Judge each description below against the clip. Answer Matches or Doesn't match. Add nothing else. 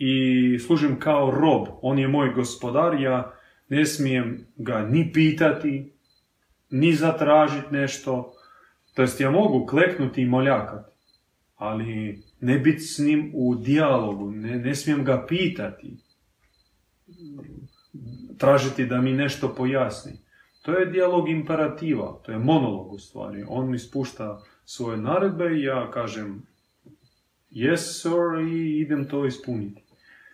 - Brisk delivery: Doesn't match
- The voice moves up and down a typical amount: Matches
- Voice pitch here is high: Doesn't match